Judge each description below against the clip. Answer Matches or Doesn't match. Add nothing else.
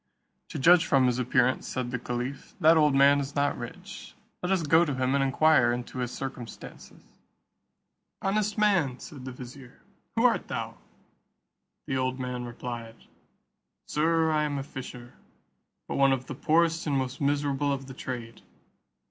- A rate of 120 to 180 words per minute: Matches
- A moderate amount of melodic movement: Matches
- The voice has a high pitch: Doesn't match